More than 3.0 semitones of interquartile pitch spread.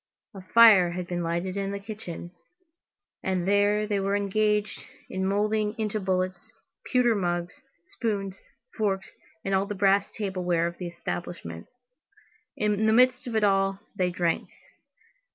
No: narrow, 2.6 semitones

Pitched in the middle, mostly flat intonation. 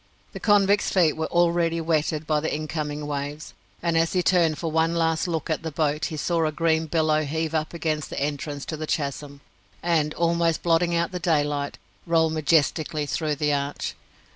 Yes: medium, 160 Hz; narrow, 1.9 semitones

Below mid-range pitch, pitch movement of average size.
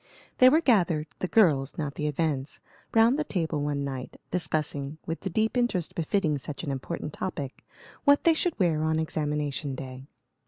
No: medium, 155 Hz; average, 4.9 semitones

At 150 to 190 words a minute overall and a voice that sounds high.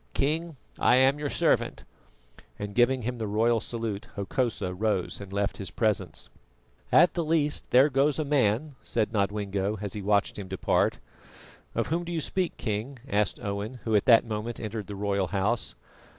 No: average, 175 wpm; low, 110 Hz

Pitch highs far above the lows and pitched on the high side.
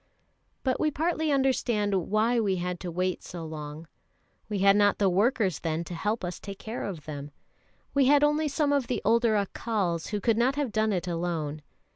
Yes: wide, 5.7 semitones; high, 205 Hz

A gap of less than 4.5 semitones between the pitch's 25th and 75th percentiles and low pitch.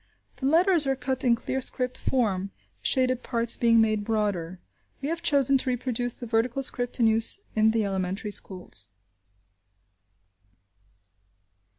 No: average, 3.4 semitones; high, 235 Hz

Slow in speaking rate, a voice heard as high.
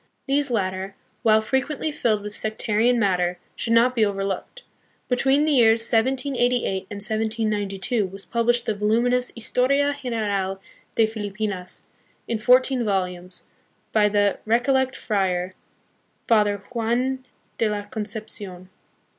Yes: slow, 125 wpm; high, 220 Hz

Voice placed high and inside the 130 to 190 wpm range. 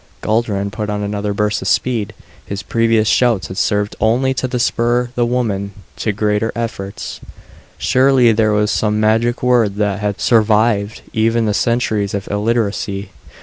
No: low, 110 Hz; average, 150 wpm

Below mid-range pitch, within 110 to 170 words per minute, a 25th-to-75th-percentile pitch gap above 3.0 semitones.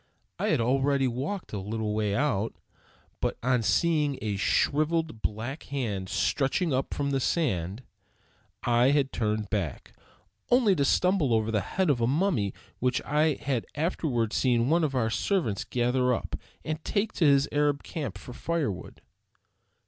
Yes: low, 130 Hz; average, 155 wpm; average, 5.2 semitones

